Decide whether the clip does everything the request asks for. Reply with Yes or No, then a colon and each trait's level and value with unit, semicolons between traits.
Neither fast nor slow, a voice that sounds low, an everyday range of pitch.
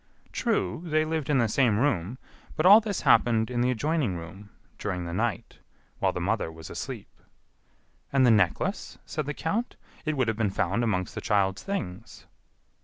No: average, 180 wpm; low, 115 Hz; wide, 7.8 semitones